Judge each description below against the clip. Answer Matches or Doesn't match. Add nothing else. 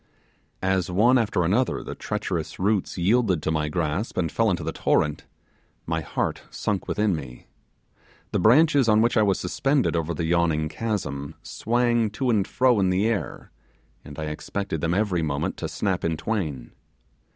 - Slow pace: Doesn't match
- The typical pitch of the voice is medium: Doesn't match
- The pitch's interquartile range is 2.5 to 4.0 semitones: Doesn't match